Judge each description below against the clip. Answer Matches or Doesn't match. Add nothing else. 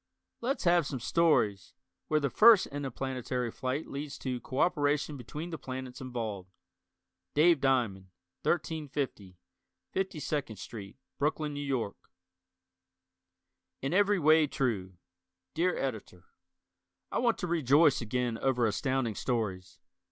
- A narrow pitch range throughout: Doesn't match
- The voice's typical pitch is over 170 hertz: Doesn't match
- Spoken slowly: Matches